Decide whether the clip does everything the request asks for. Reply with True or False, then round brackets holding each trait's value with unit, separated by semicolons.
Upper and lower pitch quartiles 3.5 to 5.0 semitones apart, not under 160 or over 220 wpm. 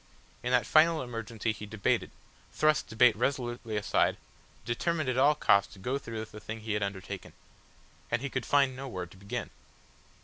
True (4.4 semitones; 180 wpm)